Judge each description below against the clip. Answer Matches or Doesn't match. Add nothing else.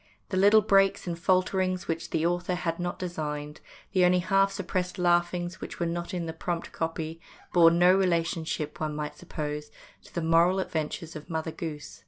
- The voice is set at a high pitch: Doesn't match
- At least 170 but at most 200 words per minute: Matches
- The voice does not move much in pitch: Matches